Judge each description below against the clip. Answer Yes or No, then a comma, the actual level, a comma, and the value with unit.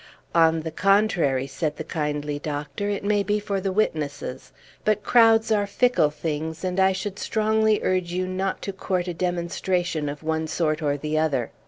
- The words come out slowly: No, average, 180 wpm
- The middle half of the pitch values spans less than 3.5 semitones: No, average, 4.5 semitones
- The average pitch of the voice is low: No, medium, 175 Hz